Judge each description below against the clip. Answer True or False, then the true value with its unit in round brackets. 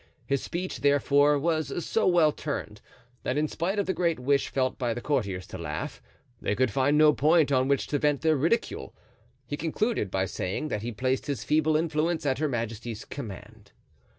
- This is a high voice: False (140 Hz)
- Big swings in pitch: False (4.6 semitones)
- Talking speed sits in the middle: True (190 wpm)